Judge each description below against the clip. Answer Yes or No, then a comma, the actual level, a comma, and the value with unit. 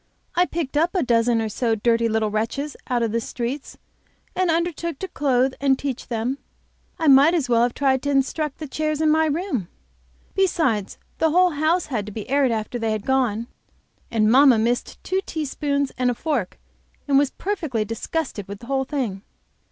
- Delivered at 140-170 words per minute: No, average, 190 wpm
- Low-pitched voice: No, very high, 265 Hz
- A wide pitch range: No, average, 5.0 semitones